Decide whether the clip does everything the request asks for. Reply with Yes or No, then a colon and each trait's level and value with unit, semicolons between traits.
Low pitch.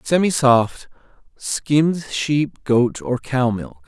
Yes: low, 130 Hz